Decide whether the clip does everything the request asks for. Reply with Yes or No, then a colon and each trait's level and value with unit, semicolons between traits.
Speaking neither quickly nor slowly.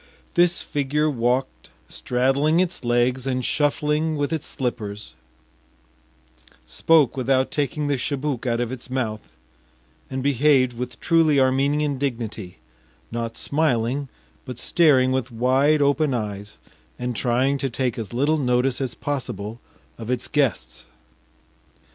No: slow, 125 wpm